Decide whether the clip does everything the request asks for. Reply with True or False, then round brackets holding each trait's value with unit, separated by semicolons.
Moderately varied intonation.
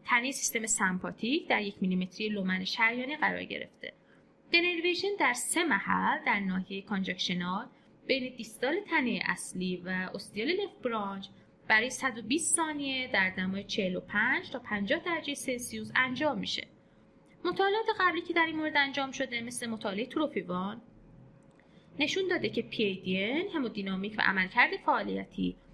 False (7.7 semitones)